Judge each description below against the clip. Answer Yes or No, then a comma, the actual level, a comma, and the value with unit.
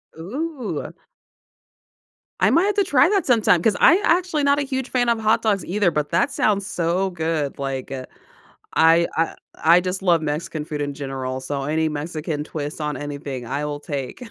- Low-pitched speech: No, medium, 165 Hz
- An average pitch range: No, wide, 7.7 semitones